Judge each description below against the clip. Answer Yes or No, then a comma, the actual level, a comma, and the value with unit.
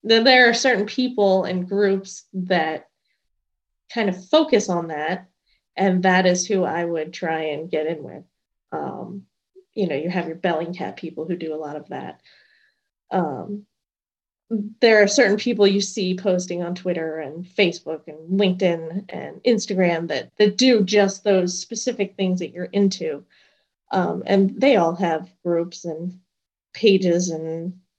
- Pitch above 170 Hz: Yes, medium, 185 Hz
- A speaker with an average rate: Yes, average, 155 wpm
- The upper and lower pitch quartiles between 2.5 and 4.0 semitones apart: Yes, average, 3.3 semitones